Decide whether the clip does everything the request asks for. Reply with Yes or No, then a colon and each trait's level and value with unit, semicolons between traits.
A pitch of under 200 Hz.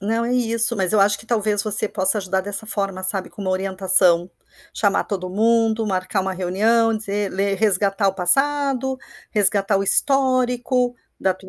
No: high, 205 Hz